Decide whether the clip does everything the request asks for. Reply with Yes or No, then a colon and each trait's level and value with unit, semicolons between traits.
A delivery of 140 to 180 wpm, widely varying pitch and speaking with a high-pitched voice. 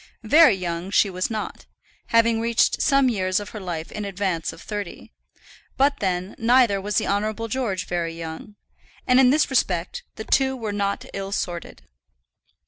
No: average, 165 wpm; average, 3.9 semitones; high, 205 Hz